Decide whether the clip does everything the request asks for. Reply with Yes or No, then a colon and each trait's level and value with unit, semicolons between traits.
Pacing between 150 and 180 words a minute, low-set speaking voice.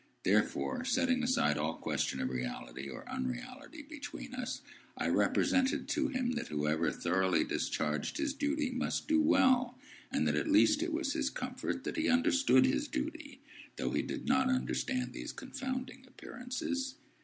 No: average, 155 wpm; very high, 260 Hz